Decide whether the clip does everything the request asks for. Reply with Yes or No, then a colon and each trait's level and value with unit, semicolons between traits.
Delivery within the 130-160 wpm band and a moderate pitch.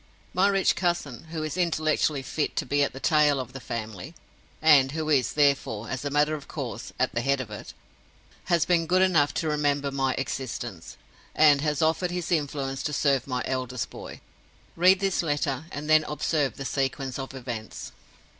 No: average, 185 wpm; medium, 145 Hz